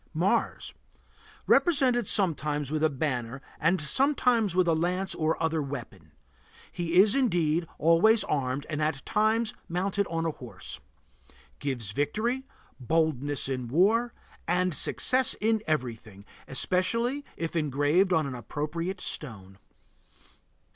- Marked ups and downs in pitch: Yes, wide, 5.7 semitones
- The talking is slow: Yes, slow, 120 wpm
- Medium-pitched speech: Yes, medium, 165 Hz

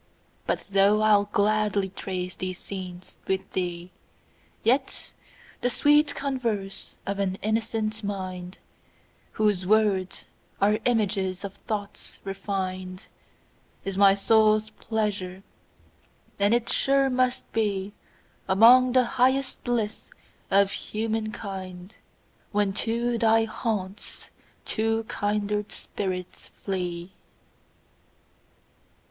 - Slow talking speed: Yes, slow, 90 wpm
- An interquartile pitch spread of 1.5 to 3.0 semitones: Yes, average, 2.7 semitones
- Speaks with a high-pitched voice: Yes, high, 205 Hz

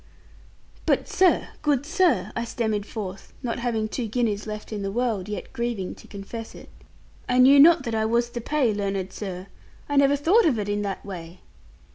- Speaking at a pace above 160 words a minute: Yes, average, 190 wpm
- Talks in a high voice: Yes, high, 225 Hz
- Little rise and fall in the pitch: No, average, 3.9 semitones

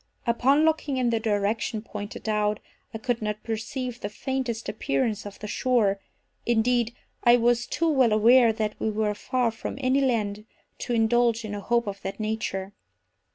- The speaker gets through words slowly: No, average, 165 wpm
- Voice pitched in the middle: No, high, 225 Hz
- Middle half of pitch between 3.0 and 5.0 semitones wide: No, narrow, 2.5 semitones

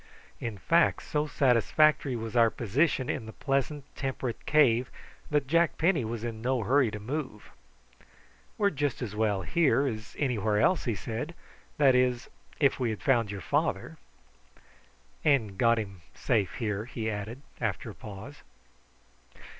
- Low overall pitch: Yes, low, 125 Hz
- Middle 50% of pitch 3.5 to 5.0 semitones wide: Yes, average, 4.6 semitones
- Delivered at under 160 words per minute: Yes, average, 150 wpm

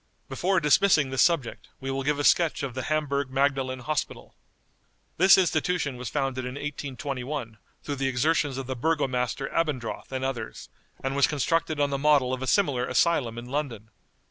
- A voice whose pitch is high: No, low, 135 Hz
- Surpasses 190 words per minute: No, average, 170 wpm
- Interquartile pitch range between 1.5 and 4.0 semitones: Yes, average, 2.7 semitones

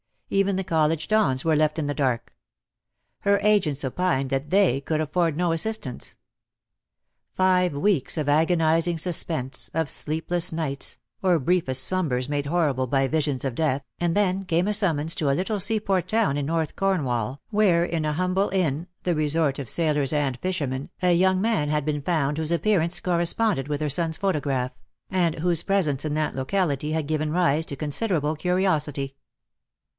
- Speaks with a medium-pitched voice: Yes, medium, 160 Hz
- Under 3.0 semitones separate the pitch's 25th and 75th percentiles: No, average, 4.1 semitones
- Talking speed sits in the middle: Yes, average, 170 wpm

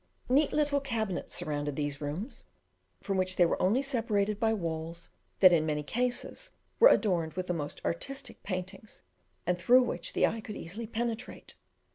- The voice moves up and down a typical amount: No, wide, 6.0 semitones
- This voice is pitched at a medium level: No, high, 195 Hz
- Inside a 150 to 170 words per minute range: Yes, average, 165 wpm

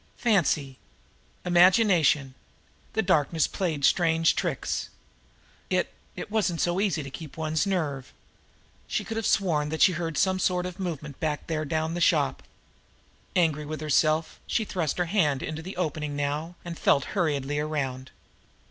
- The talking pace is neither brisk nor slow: Yes, average, 155 wpm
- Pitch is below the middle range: No, medium, 160 Hz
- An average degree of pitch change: Yes, average, 3.3 semitones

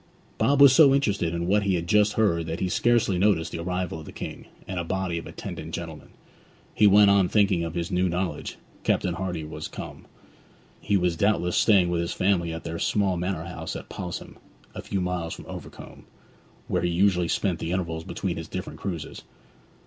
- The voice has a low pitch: Yes, very low, 90 Hz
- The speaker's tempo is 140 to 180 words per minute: No, average, 200 wpm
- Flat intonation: No, average, 3.0 semitones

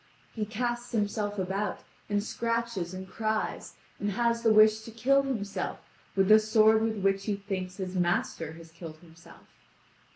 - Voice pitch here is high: Yes, high, 210 Hz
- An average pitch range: Yes, average, 3.0 semitones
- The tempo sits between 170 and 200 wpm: No, average, 160 wpm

